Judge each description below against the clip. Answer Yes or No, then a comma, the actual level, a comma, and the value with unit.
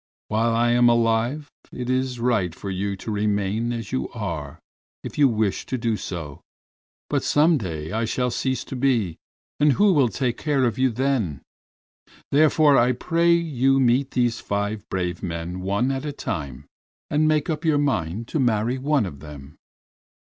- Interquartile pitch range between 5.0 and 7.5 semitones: Yes, average, 5.3 semitones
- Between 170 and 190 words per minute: Yes, average, 175 wpm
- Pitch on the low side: Yes, low, 120 Hz